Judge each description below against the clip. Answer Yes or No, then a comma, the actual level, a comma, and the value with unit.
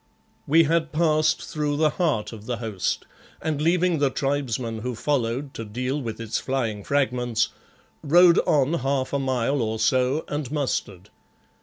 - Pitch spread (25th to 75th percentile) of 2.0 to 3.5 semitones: No, average, 4.6 semitones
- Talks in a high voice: No, low, 135 Hz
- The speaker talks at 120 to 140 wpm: No, average, 155 wpm